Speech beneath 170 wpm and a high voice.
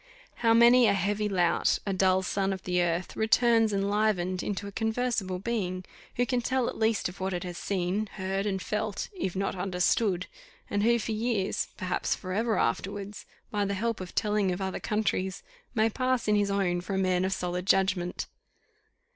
No: average, 185 wpm; high, 195 Hz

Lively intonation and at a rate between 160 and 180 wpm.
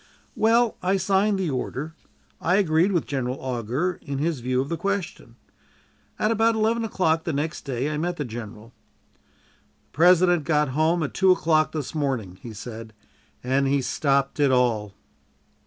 Yes: wide, 5.9 semitones; average, 165 wpm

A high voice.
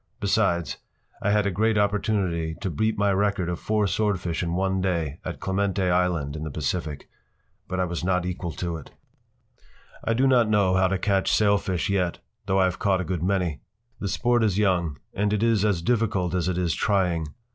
No: very low, 95 Hz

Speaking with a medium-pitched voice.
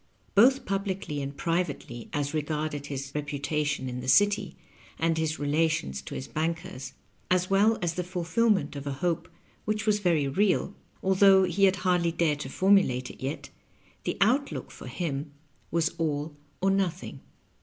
Yes: medium, 165 Hz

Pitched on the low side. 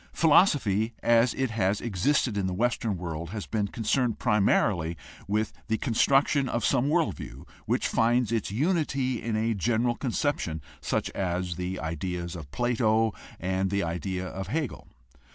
Yes: low, 110 Hz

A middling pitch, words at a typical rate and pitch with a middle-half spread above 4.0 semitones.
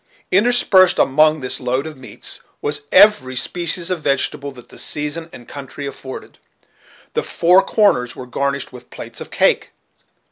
Yes: medium, 145 Hz; average, 150 wpm; average, 5.2 semitones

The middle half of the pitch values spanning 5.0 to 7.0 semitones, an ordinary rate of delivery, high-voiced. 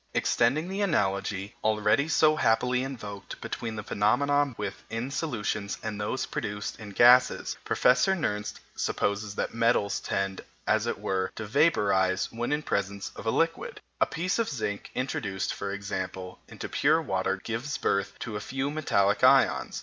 No: wide, 5.4 semitones; average, 160 wpm; low, 110 Hz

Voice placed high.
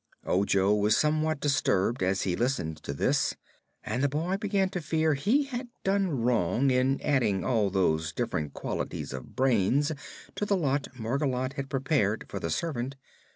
No: low, 130 Hz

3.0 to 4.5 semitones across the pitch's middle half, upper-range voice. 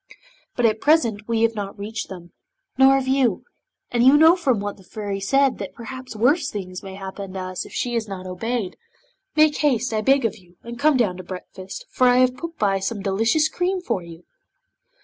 No: average, 5.3 semitones; high, 225 Hz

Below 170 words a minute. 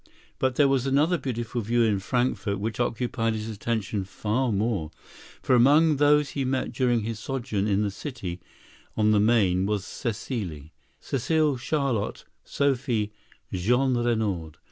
Yes: slow, 135 wpm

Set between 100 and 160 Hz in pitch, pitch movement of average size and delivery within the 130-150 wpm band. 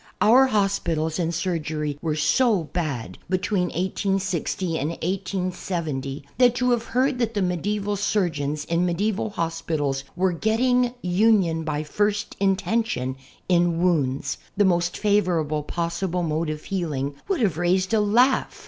No: medium, 180 Hz; average, 4.6 semitones; average, 140 wpm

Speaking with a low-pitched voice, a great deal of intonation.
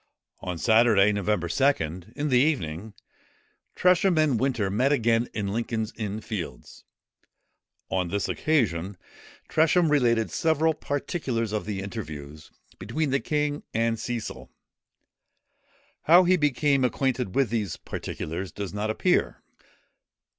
Yes: low, 115 Hz; wide, 6.3 semitones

